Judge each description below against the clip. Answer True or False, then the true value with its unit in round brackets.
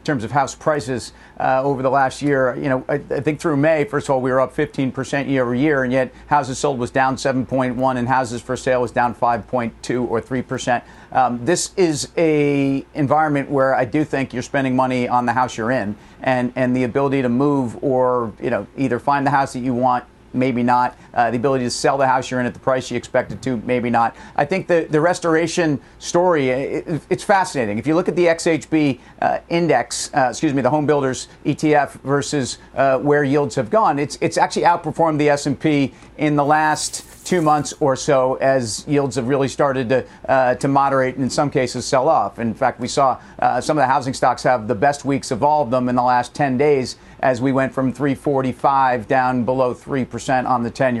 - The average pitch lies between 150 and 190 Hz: False (135 Hz)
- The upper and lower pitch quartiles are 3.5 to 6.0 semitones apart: False (2.6 semitones)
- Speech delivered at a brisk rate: True (220 wpm)